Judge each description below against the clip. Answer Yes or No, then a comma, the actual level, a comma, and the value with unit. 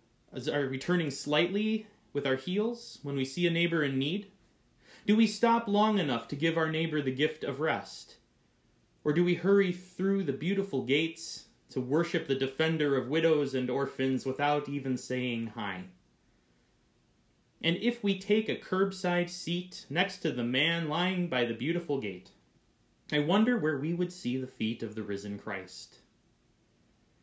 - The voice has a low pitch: No, medium, 155 Hz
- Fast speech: No, average, 165 wpm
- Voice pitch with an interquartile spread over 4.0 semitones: Yes, wide, 5.5 semitones